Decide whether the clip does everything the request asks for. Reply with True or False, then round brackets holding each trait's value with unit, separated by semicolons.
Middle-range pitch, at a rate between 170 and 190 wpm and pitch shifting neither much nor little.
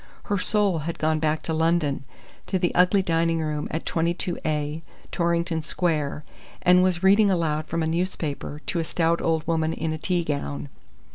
False (165 Hz; 180 wpm; 2.1 semitones)